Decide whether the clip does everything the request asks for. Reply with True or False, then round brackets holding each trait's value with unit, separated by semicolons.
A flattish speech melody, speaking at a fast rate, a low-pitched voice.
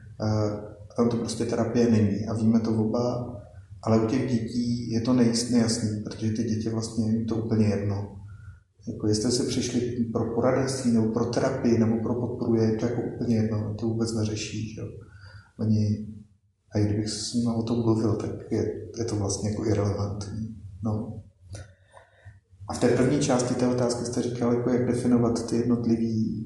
True (1.9 semitones; 180 wpm; 115 Hz)